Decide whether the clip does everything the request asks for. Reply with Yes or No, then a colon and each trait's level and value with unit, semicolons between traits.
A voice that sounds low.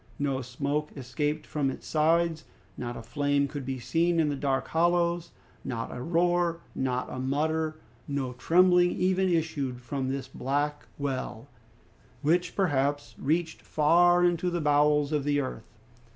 No: medium, 150 Hz